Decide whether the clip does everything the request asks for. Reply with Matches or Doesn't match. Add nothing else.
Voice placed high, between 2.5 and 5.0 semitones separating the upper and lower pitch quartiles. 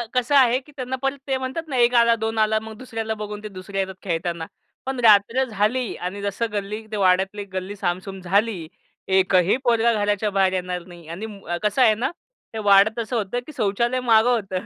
Matches